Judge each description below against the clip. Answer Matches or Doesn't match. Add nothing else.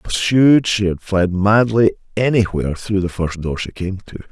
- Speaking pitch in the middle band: Doesn't match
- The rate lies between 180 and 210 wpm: Doesn't match